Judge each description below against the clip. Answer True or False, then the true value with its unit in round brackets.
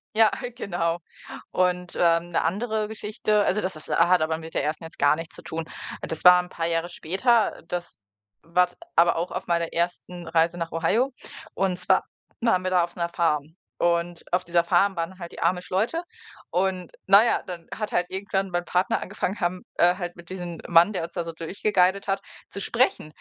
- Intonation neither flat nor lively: False (2.3 semitones)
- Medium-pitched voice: True (175 Hz)